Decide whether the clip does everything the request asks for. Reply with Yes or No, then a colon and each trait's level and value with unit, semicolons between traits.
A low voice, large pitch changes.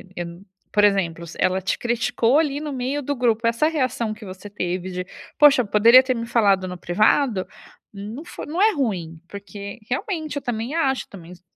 No: high, 225 Hz; wide, 5.9 semitones